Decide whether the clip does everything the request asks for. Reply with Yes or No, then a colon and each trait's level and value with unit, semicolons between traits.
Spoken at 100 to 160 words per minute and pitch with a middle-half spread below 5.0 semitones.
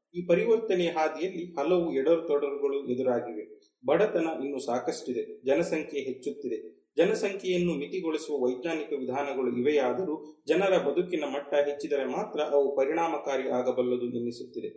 No: fast, 105 wpm; wide, 5.5 semitones